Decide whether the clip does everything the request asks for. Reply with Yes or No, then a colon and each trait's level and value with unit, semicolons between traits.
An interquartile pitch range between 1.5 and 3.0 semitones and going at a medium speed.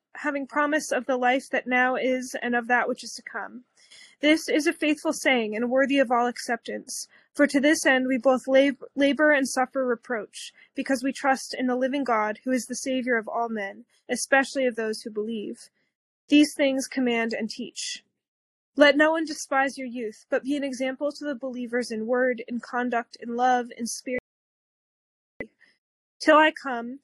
Yes: narrow, 2.5 semitones; average, 185 wpm